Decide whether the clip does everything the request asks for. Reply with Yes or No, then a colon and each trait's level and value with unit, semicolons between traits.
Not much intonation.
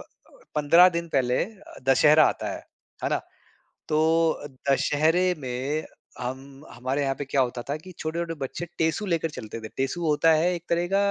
No: average, 4.0 semitones